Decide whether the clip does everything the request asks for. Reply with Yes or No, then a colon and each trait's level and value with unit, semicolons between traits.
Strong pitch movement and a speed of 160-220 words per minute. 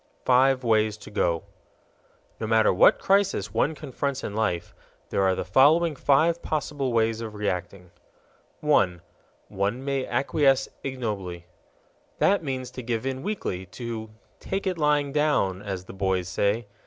No: wide, 6.1 semitones; average, 145 wpm